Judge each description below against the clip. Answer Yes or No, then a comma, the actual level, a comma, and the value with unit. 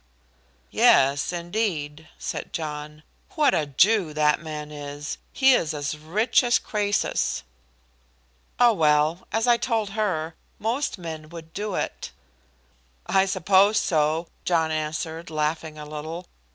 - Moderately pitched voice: Yes, medium, 160 Hz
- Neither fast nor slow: No, slow, 125 wpm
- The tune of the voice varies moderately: Yes, average, 5.0 semitones